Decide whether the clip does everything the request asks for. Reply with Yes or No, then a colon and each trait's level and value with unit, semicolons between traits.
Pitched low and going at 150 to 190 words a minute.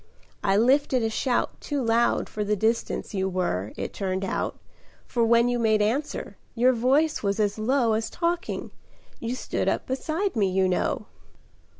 No: high, 230 Hz; average, 170 wpm